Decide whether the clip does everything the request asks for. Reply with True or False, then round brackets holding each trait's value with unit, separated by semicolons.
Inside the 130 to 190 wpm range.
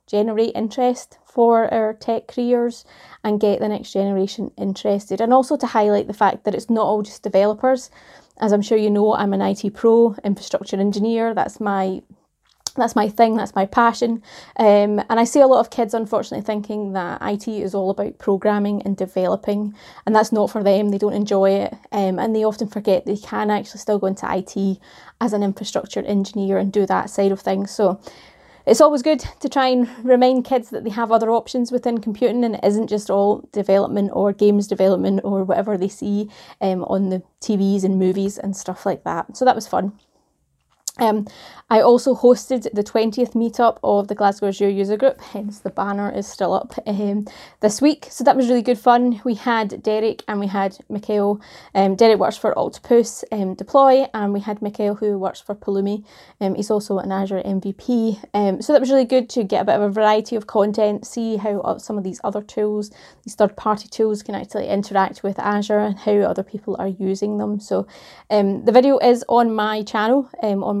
False (205 wpm)